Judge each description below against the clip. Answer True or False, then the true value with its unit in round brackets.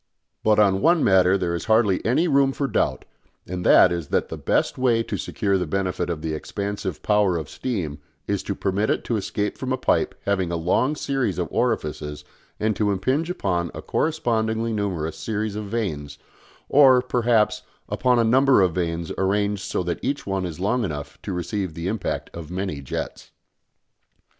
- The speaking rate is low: False (185 wpm)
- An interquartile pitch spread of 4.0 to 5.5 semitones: True (4.6 semitones)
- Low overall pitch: True (100 Hz)